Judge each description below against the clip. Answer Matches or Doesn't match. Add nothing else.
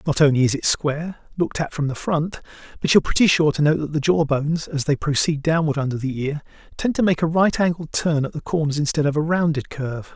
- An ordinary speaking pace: Doesn't match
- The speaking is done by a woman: Doesn't match